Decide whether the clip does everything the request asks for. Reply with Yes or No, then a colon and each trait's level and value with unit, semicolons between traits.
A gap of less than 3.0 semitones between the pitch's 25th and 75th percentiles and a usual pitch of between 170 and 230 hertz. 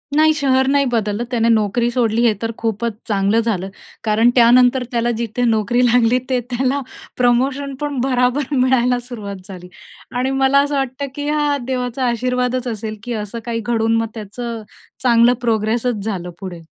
No: narrow, 2.4 semitones; high, 240 Hz